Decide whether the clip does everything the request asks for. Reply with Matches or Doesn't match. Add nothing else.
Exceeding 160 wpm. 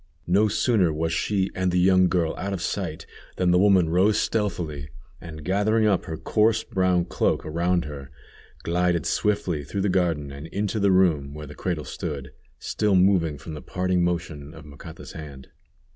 Matches